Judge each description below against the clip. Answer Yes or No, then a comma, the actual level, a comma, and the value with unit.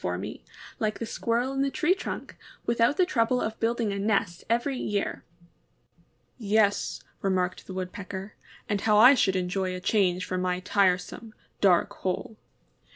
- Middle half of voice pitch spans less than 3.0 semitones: No, average, 3.7 semitones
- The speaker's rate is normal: Yes, average, 165 wpm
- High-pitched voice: Yes, high, 205 Hz